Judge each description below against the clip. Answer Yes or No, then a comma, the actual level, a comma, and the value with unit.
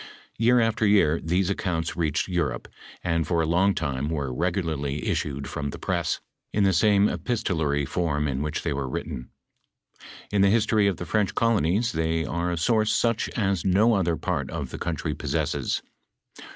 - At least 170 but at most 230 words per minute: Yes, average, 180 wpm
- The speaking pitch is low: Yes, very low, 85 Hz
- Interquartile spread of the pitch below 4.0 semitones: No, average, 4.9 semitones